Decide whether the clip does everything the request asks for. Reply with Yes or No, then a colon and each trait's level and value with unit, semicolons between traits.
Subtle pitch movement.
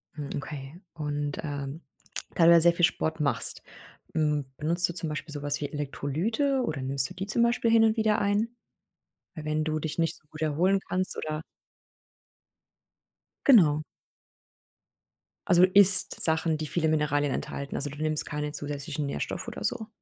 No: average, 3.7 semitones